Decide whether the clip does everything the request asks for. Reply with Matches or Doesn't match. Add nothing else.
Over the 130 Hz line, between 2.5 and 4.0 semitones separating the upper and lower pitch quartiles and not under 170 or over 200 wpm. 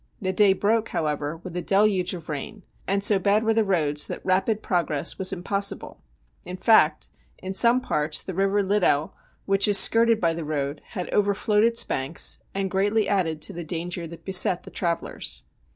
Matches